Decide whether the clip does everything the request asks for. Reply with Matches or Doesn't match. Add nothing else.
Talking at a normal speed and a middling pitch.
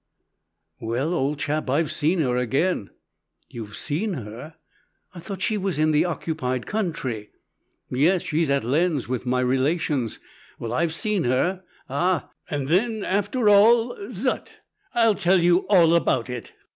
Matches